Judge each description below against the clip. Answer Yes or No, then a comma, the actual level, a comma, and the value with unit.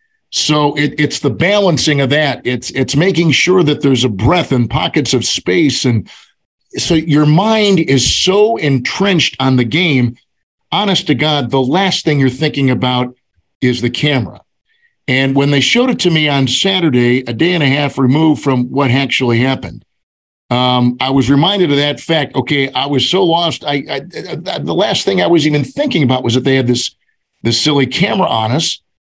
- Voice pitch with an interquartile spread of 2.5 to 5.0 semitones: Yes, average, 4.2 semitones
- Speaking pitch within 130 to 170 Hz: Yes, medium, 140 Hz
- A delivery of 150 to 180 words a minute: No, average, 190 wpm